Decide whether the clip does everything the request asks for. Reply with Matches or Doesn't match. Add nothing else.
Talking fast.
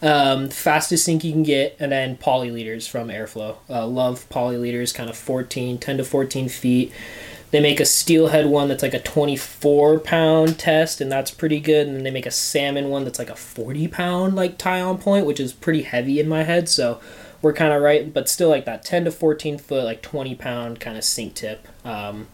Matches